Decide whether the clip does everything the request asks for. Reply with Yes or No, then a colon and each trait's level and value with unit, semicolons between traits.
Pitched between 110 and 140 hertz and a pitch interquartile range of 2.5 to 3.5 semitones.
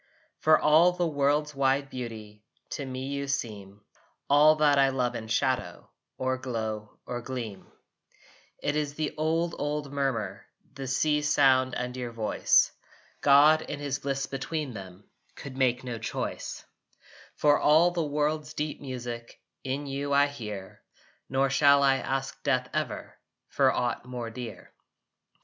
Yes: low, 135 Hz; average, 3.0 semitones